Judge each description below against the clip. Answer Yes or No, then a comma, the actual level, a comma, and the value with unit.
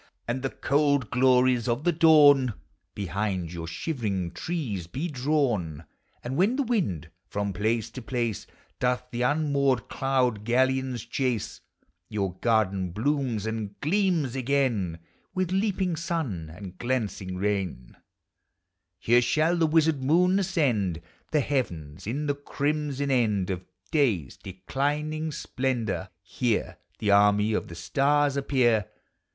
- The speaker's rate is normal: No, slow, 125 wpm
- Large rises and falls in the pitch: Yes, wide, 6.1 semitones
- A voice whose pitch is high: No, low, 125 Hz